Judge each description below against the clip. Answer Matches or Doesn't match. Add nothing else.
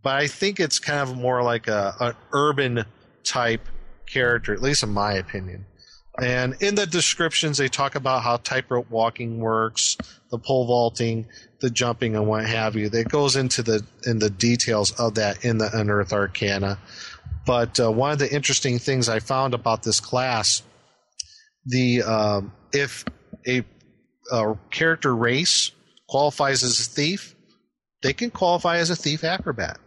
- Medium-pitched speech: Doesn't match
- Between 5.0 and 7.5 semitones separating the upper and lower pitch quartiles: Doesn't match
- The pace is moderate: Matches